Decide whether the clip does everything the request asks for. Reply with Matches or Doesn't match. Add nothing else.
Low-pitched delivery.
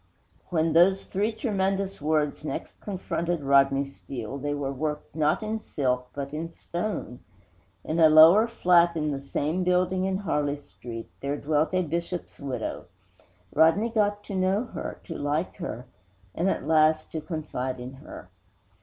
Doesn't match